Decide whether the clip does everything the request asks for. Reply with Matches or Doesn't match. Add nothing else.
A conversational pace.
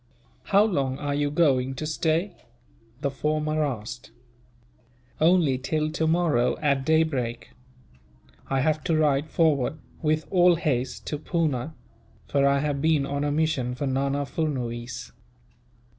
Doesn't match